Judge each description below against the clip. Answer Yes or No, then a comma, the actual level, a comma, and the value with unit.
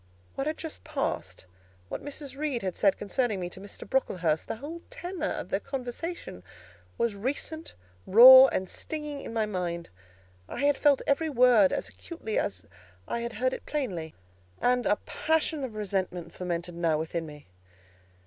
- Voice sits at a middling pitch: No, high, 235 Hz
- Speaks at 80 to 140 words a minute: No, average, 165 wpm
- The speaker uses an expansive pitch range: Yes, wide, 7.7 semitones